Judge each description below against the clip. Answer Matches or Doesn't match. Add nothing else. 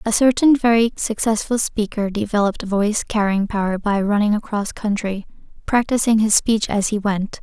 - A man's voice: Doesn't match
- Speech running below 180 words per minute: Matches